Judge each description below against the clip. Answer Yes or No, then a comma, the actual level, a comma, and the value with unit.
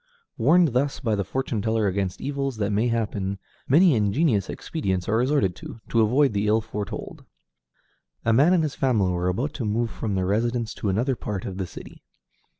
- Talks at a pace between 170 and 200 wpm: Yes, average, 190 wpm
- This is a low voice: Yes, low, 110 Hz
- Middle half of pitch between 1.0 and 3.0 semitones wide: No, average, 4.9 semitones